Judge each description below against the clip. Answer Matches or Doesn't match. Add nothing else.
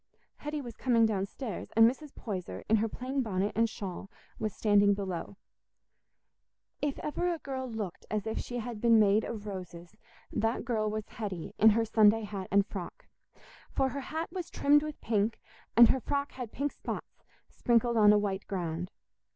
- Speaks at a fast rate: Doesn't match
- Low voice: Doesn't match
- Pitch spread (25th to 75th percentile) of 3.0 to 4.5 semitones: Matches